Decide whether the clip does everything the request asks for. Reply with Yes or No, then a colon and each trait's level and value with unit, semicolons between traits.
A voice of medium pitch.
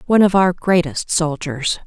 Yes: medium, 170 Hz